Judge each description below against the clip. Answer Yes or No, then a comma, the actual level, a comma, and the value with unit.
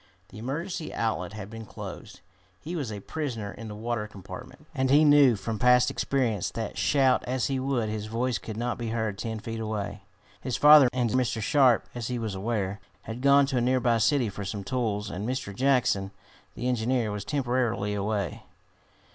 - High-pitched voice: No, low, 115 Hz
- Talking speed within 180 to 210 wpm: Yes, average, 190 wpm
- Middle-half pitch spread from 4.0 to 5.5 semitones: No, average, 3.5 semitones